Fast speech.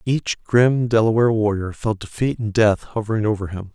No: average, 175 wpm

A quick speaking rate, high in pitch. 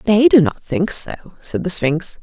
Yes: fast, 215 wpm; high, 205 Hz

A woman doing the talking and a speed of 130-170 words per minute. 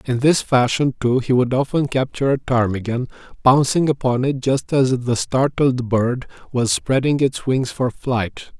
No: male; average, 165 wpm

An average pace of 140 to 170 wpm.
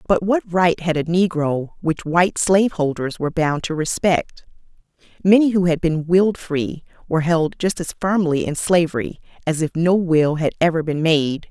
No: average, 185 wpm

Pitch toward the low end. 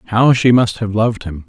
Yes: low, 110 Hz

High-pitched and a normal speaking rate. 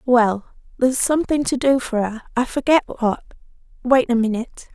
Yes: high, 245 Hz; average, 165 wpm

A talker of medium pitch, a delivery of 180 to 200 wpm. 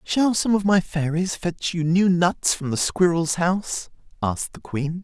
Yes: medium, 175 Hz; average, 190 wpm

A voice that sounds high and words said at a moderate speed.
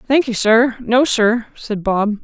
Yes: high, 230 Hz; average, 160 wpm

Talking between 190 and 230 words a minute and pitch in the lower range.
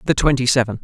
Yes: fast, 215 wpm; low, 125 Hz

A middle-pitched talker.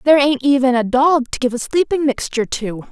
No: very high, 265 Hz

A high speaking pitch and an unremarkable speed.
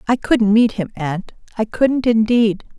Yes: high, 220 Hz; average, 170 wpm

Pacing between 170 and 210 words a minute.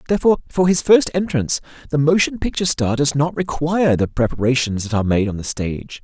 Yes: average, 200 wpm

